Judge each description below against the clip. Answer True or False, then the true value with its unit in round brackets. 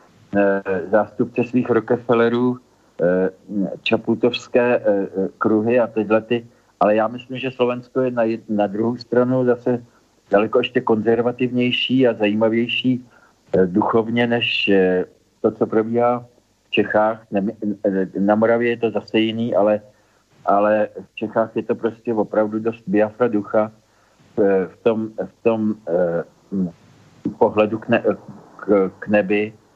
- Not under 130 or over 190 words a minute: False (115 wpm)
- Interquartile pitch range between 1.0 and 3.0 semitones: True (2.4 semitones)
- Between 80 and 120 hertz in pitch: True (110 Hz)